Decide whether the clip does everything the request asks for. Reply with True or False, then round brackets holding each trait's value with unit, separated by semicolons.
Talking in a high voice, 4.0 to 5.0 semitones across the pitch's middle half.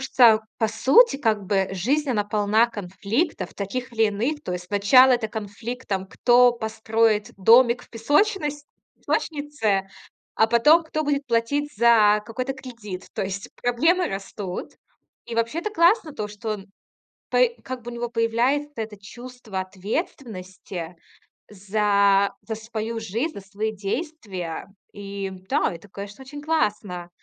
True (225 Hz; 4.6 semitones)